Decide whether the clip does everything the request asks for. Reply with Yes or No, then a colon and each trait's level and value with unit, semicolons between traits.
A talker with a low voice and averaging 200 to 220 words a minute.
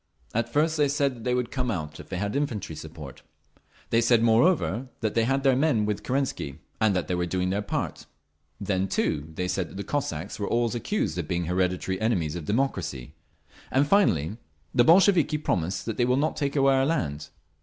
Yes: low, 110 Hz; fast, 205 wpm